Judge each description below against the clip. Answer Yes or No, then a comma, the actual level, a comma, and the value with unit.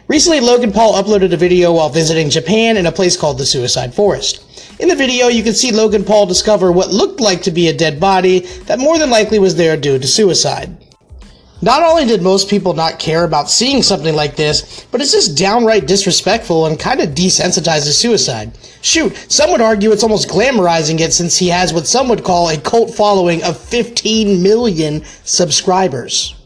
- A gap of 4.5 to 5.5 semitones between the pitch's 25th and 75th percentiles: Yes, average, 5.2 semitones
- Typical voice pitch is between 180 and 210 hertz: Yes, high, 190 Hz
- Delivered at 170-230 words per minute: Yes, average, 195 wpm